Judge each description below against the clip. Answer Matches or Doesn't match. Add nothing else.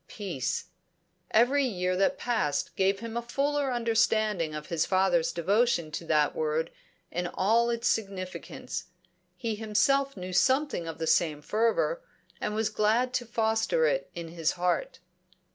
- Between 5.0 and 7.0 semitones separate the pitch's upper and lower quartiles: Matches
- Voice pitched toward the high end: Matches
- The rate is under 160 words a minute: Matches